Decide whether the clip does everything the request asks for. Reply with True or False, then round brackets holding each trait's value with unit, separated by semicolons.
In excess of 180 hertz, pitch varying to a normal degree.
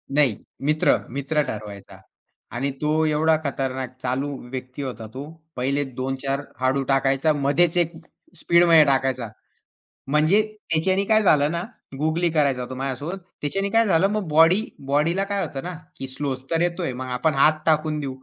False (150 Hz; 3.7 semitones)